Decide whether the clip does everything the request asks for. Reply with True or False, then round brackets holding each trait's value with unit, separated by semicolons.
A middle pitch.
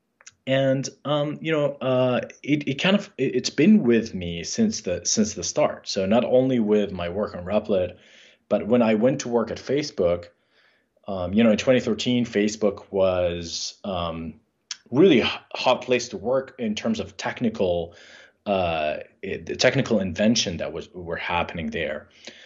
False (120 Hz)